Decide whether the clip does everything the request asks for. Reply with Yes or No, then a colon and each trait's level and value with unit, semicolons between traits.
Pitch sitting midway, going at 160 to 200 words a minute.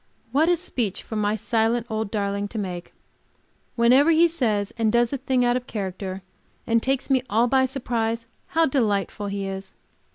No: high, 230 Hz; average, 175 wpm